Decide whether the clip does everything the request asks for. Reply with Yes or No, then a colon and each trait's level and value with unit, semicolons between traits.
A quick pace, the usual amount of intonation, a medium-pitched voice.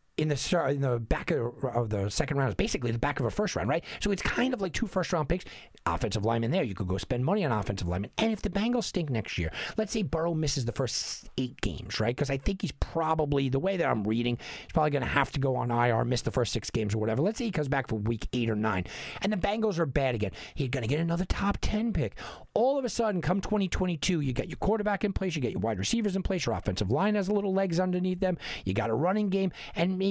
No: fast, 275 wpm; wide, 8.4 semitones; medium, 145 Hz